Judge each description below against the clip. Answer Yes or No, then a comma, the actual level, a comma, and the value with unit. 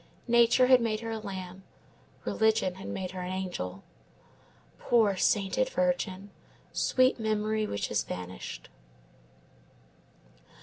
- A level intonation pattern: No, average, 3.8 semitones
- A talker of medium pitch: No, high, 210 Hz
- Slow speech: Yes, slow, 115 wpm